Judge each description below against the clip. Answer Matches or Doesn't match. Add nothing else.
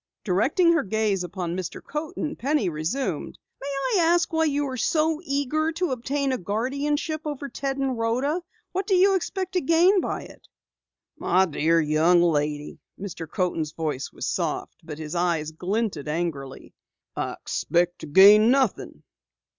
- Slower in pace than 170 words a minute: Matches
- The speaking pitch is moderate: Doesn't match